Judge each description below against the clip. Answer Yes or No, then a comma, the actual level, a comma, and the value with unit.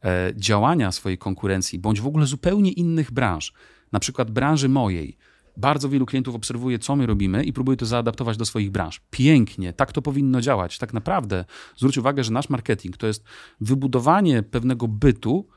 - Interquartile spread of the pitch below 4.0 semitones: No, average, 5.0 semitones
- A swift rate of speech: Yes, fast, 170 wpm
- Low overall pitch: Yes, low, 125 Hz